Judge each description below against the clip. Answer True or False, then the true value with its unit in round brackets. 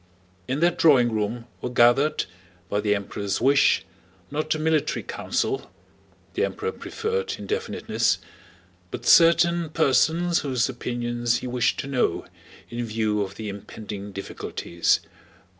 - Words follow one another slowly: True (125 wpm)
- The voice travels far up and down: True (6.6 semitones)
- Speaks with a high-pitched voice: False (125 Hz)